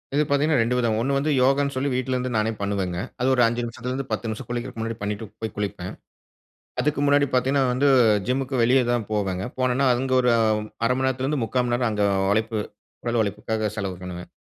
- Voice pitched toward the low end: Yes, low, 120 Hz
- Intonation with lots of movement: No, average, 3.5 semitones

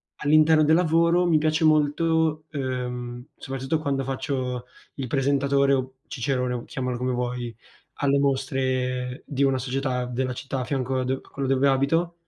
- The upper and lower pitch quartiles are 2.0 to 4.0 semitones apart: Yes, narrow, 2.5 semitones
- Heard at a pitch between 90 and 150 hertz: Yes, low, 135 Hz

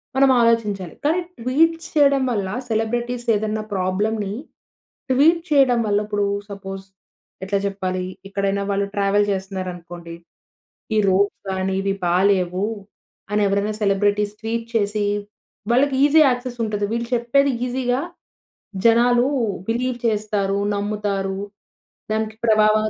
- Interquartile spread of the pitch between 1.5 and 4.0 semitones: Yes, average, 3.4 semitones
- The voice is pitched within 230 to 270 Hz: No, high, 210 Hz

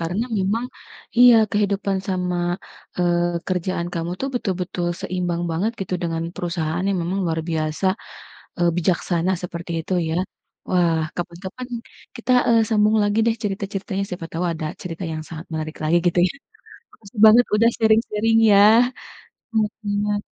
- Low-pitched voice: No, medium, 185 Hz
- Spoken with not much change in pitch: No, average, 3.4 semitones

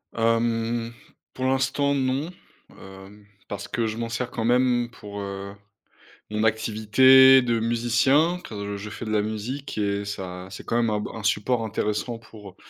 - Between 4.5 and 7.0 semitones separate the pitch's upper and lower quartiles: No, average, 3.0 semitones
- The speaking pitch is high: No, low, 115 Hz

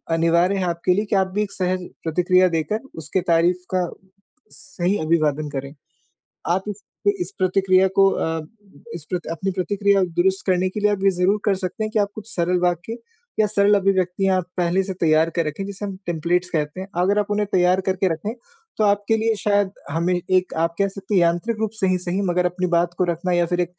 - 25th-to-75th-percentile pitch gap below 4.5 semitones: Yes, narrow, 2.5 semitones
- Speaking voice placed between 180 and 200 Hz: Yes, medium, 185 Hz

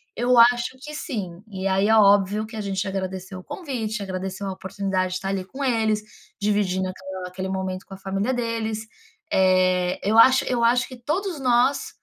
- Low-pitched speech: No, high, 205 Hz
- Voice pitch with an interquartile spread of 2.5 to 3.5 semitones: No, average, 4.0 semitones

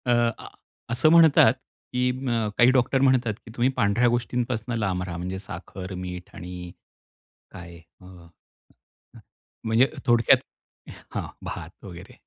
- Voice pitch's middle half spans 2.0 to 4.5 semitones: No, average, 5.1 semitones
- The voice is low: Yes, low, 115 Hz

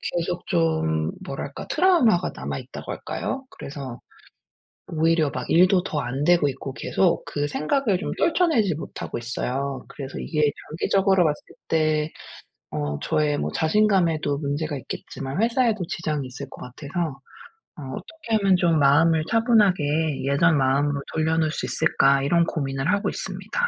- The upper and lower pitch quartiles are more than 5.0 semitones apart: No, average, 4.6 semitones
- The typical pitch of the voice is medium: Yes, medium, 155 Hz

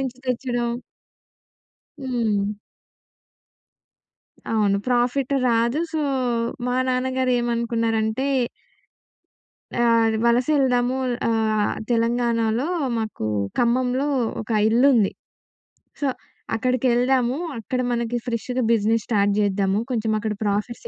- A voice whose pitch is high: Yes, high, 235 Hz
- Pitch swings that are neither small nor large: No, narrow, 2.3 semitones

